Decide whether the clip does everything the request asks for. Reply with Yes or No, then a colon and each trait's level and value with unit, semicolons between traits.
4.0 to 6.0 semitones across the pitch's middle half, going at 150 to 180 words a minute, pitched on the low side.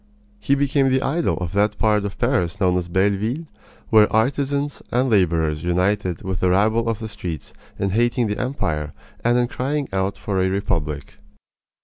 Yes: average, 5.2 semitones; average, 170 wpm; low, 105 Hz